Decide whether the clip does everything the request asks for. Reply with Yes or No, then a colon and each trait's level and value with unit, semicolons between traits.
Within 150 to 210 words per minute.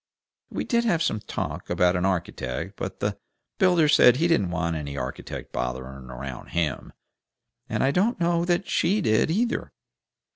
Yes: average, 160 wpm